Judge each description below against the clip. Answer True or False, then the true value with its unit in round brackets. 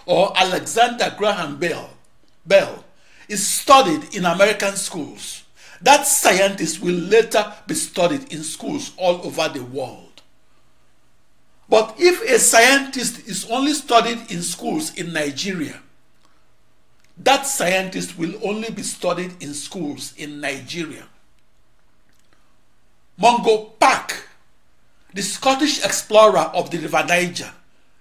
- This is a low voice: False (200 Hz)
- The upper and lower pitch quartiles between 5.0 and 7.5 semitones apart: True (5.5 semitones)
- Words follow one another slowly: True (110 wpm)